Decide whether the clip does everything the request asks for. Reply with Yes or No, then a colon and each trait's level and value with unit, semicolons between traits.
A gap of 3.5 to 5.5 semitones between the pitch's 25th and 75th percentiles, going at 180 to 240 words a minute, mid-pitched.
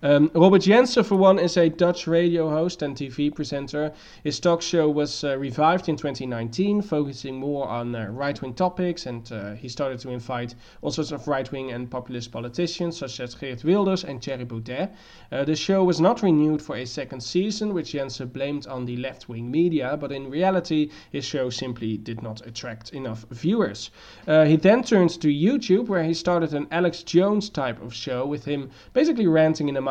Yes: average, 5.1 semitones; average, 200 wpm; medium, 150 Hz